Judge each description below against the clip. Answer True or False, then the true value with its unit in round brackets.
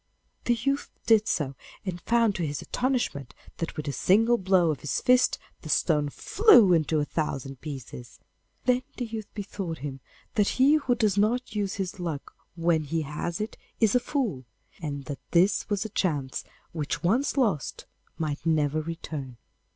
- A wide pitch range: True (7.0 semitones)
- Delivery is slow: False (170 wpm)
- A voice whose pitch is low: False (175 Hz)